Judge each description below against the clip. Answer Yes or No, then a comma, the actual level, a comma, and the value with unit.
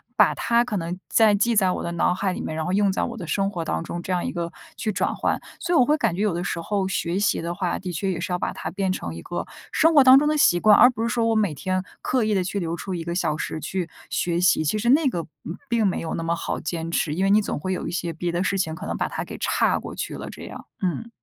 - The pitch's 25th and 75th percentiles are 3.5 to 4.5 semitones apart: Yes, average, 3.9 semitones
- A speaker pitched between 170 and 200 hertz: Yes, medium, 185 Hz